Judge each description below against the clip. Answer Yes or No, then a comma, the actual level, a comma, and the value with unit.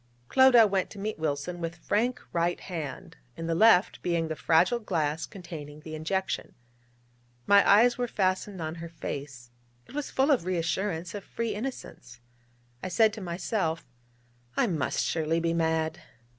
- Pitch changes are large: No, average, 4.3 semitones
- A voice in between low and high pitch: Yes, medium, 175 Hz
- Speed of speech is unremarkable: Yes, average, 155 wpm